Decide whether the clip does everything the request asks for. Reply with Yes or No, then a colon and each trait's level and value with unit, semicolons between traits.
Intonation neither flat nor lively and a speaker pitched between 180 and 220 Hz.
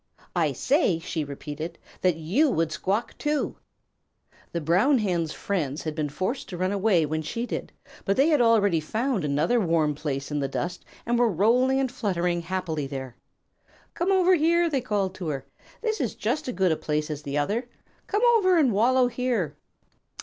No: wide, 8.1 semitones; high, 190 Hz